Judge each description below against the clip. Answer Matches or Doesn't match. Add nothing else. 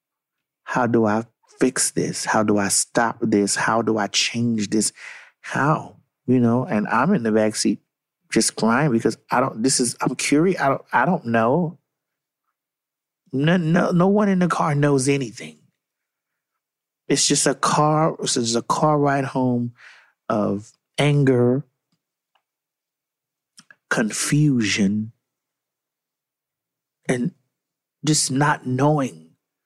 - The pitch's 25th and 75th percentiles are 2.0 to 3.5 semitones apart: Doesn't match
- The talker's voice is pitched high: Doesn't match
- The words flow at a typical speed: Doesn't match